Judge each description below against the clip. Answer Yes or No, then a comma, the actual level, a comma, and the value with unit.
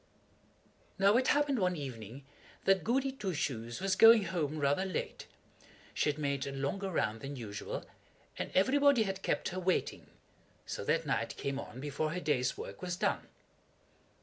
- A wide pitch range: Yes, wide, 6.0 semitones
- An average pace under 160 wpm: No, average, 165 wpm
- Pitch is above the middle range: No, medium, 170 Hz